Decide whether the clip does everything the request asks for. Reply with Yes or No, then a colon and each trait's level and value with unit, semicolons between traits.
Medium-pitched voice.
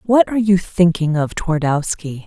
Yes: medium, 175 Hz